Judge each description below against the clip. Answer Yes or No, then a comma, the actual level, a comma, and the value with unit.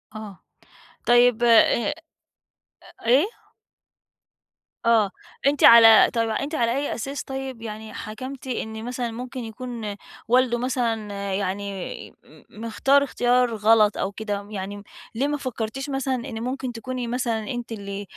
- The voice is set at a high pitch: Yes, high, 235 Hz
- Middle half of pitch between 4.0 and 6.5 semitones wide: No, average, 2.8 semitones